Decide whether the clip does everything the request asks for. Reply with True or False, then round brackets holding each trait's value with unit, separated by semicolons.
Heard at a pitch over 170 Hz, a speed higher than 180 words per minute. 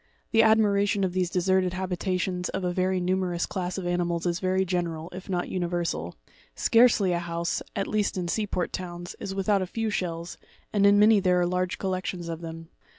True (185 Hz; 195 wpm)